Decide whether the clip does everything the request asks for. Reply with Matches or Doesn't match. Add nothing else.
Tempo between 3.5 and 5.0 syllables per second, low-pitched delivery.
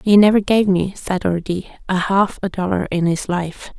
Doesn't match